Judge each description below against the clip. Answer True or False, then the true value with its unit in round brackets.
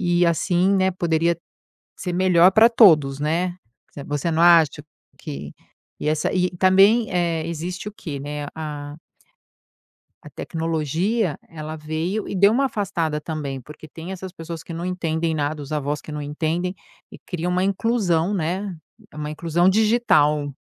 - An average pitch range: True (3.4 semitones)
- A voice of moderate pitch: True (170 Hz)